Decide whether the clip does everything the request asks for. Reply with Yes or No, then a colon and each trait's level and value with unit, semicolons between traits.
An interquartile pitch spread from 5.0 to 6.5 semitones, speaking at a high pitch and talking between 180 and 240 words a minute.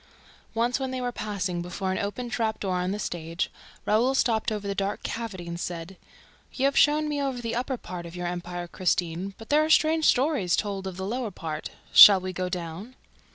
Yes: wide, 5.5 semitones; high, 205 Hz; average, 200 wpm